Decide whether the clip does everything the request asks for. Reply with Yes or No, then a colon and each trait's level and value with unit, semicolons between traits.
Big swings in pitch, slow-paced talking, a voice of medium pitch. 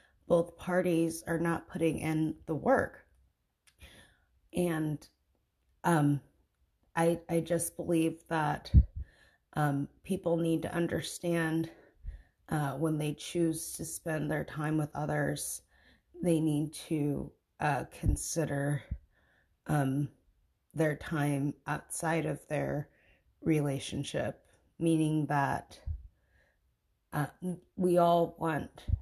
Yes: wide, 8.5 semitones; slow, 100 wpm; medium, 150 Hz